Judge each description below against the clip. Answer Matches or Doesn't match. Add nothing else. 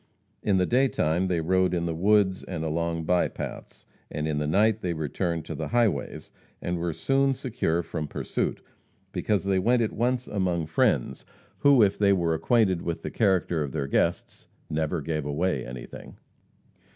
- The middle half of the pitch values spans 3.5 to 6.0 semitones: Matches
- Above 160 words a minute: Matches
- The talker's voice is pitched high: Doesn't match